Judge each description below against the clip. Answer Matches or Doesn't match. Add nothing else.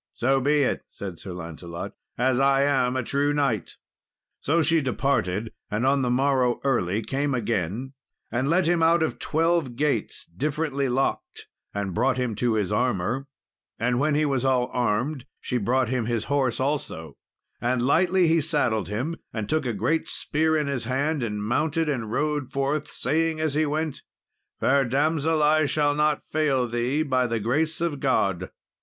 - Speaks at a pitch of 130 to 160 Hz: Matches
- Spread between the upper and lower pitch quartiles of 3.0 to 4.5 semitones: Matches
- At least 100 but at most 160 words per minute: Doesn't match